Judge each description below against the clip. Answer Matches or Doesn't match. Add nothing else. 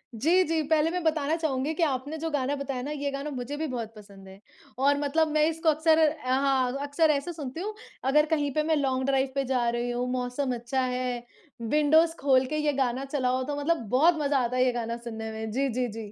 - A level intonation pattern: Doesn't match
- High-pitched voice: Matches